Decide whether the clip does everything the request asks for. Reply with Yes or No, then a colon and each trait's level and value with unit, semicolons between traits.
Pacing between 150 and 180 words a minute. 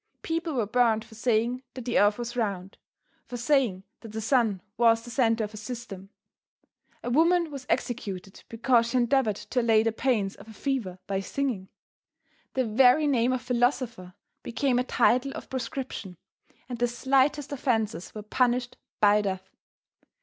Yes: average, 165 wpm